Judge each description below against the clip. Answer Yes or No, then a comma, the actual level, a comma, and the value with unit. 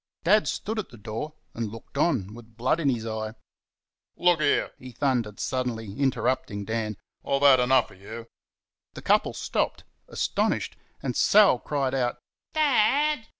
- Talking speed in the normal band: Yes, average, 150 wpm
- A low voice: Yes, low, 130 Hz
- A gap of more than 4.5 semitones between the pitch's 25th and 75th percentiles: Yes, wide, 5.4 semitones